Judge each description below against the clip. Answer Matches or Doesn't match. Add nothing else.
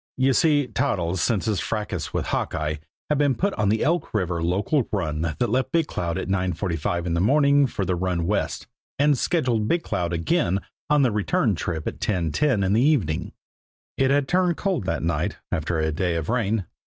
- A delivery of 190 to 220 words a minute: Matches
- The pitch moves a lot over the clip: Matches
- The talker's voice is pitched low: Matches